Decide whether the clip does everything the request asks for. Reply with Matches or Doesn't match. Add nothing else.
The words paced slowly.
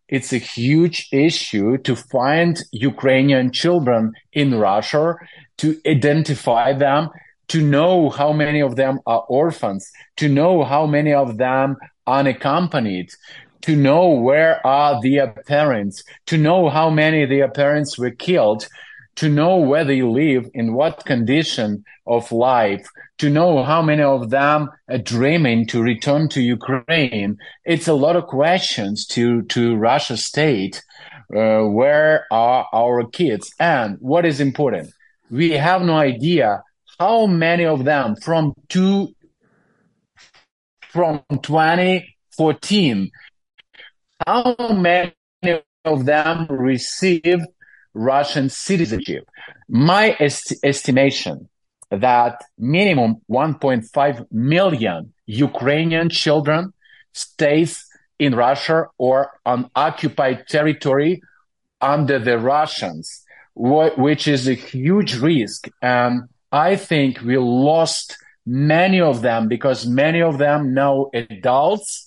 Matches